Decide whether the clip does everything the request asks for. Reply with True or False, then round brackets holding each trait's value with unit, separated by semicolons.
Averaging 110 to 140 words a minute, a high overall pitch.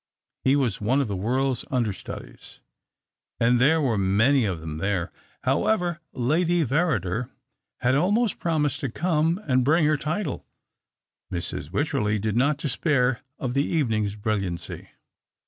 False (135 wpm; 130 Hz)